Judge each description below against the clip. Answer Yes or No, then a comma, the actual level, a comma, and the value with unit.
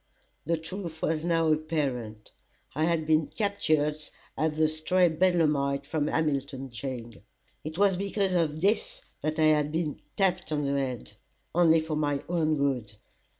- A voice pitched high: No, medium, 155 Hz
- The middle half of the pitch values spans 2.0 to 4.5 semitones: Yes, average, 2.8 semitones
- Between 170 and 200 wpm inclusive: No, average, 150 wpm